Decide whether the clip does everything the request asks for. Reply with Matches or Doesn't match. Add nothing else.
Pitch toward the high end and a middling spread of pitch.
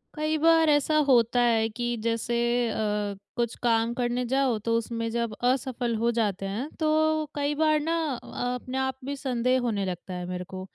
Matches